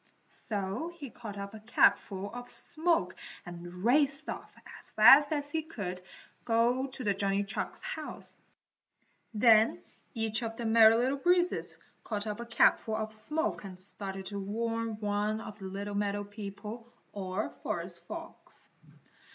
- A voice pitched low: No, high, 220 Hz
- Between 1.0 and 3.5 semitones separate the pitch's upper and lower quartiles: Yes, average, 3.2 semitones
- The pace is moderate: Yes, average, 145 wpm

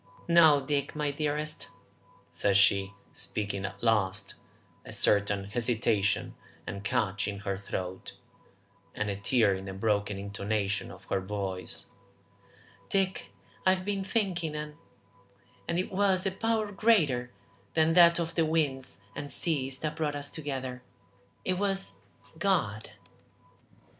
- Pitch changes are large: Yes, wide, 8.8 semitones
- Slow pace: Yes, slow, 130 wpm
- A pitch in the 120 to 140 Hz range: Yes, low, 135 Hz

